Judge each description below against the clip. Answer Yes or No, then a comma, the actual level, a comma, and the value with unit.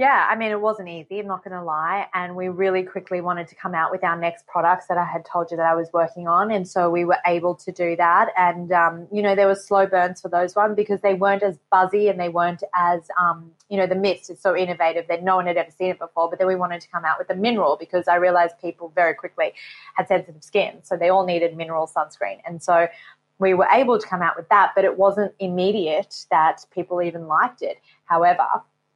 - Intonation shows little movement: Yes, narrow, 2.1 semitones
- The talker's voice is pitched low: No, medium, 180 Hz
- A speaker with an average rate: No, fast, 250 wpm